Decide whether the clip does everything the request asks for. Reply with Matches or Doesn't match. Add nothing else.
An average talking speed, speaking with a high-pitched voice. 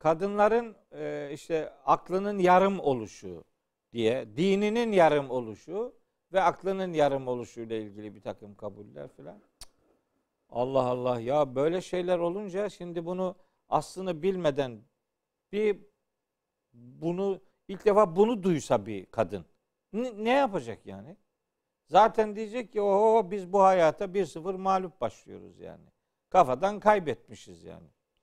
Doesn't match